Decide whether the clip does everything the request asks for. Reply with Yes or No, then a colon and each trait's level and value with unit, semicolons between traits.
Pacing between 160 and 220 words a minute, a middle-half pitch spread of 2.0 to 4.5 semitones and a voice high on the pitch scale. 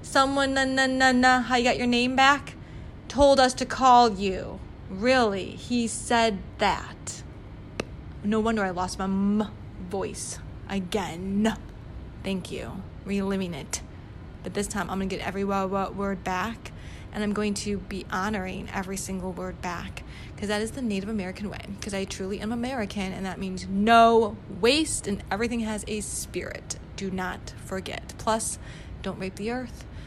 Yes: average, 170 wpm; average, 3.7 semitones; high, 205 Hz